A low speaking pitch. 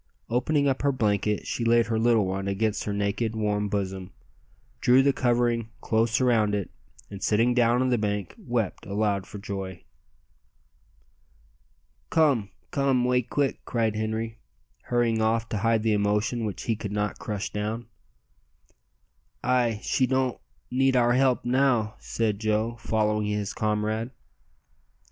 Yes: low, 110 Hz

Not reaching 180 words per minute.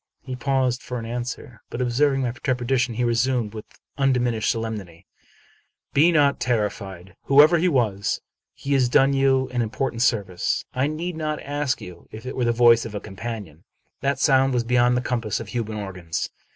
No: average, 185 wpm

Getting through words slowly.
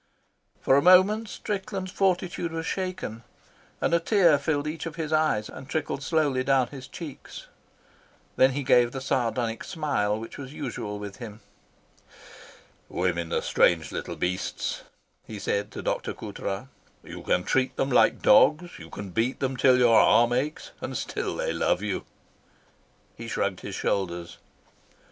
No: average, 155 wpm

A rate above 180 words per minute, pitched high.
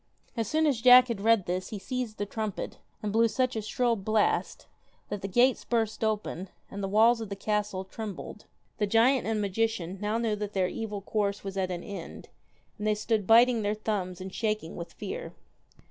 Yes: average, 200 wpm; high, 215 Hz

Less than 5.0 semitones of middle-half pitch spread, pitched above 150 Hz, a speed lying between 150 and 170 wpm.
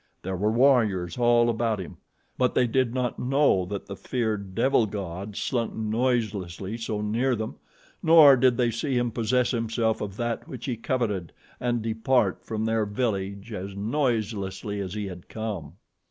No: average, 3.4 semitones; low, 110 Hz; average, 165 wpm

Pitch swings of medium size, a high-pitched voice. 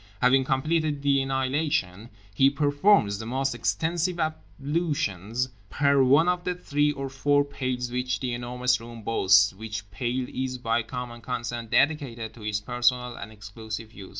No: average, 3.9 semitones; low, 125 Hz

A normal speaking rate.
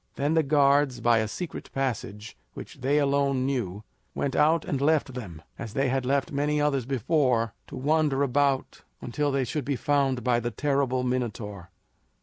Yes: average, 170 wpm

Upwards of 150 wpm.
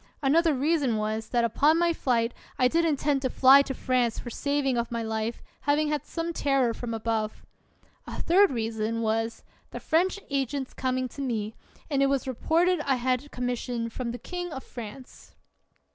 Yes: average, 180 wpm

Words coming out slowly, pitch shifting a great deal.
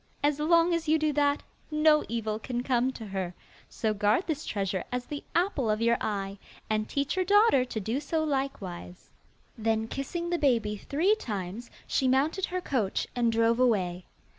No: average, 180 wpm; wide, 6.1 semitones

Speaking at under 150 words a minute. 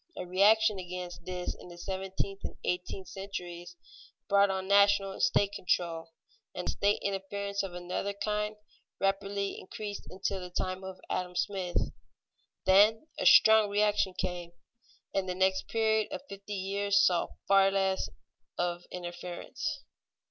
Yes: average, 140 wpm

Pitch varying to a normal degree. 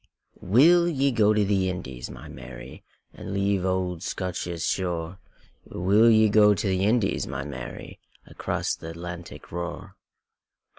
Yes: average, 3.4 semitones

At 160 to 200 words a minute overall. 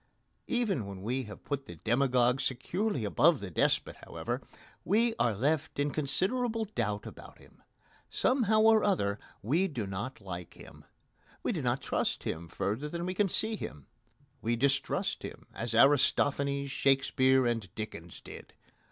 No: average, 150 wpm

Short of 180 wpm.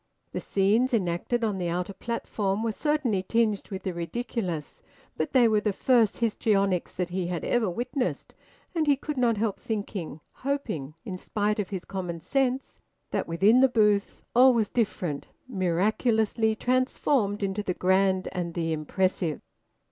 Yes: average, 155 wpm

